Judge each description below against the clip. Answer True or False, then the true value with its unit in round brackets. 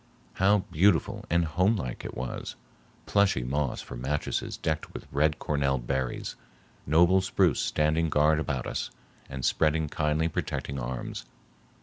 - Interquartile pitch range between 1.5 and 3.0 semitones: False (3.6 semitones)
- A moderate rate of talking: False (130 wpm)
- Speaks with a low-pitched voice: True (75 Hz)